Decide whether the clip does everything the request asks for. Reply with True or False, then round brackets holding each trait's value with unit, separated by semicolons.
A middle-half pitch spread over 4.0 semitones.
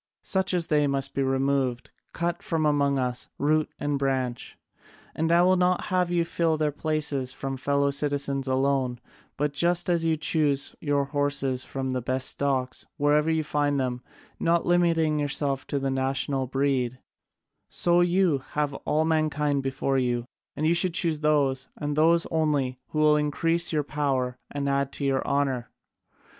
False (2.7 semitones)